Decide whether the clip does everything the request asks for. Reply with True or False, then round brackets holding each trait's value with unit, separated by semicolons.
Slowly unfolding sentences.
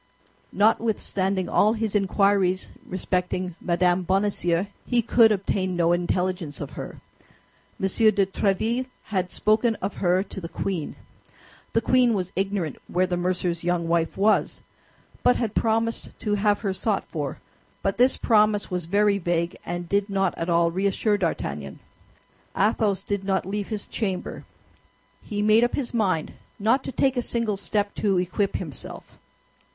False (150 wpm)